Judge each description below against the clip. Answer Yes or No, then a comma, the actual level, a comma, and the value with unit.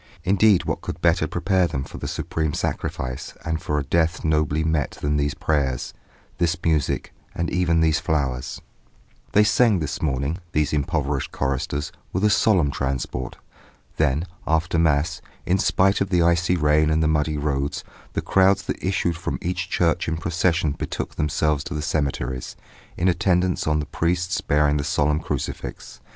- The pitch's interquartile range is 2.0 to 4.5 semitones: Yes, average, 3.2 semitones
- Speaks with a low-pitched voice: Yes, very low, 80 Hz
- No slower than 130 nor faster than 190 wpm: Yes, average, 165 wpm